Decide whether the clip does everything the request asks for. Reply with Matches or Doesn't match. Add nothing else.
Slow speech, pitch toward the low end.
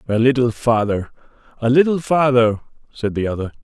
Matches